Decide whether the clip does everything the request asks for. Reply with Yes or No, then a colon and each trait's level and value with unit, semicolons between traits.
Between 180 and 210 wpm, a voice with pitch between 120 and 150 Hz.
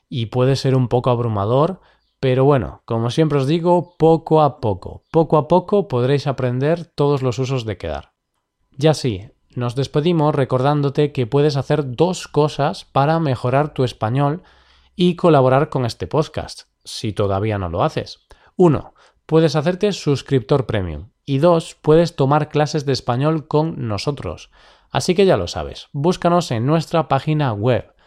No: average, 155 wpm; medium, 140 Hz